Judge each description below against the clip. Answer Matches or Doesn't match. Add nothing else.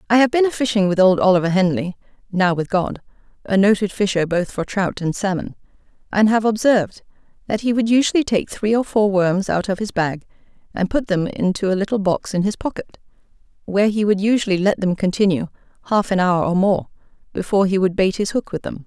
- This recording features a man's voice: Doesn't match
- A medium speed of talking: Doesn't match